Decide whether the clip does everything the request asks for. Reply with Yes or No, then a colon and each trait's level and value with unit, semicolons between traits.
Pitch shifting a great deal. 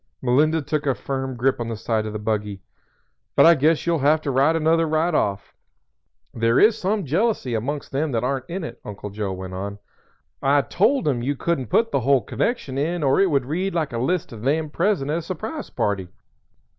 Yes: wide, 5.8 semitones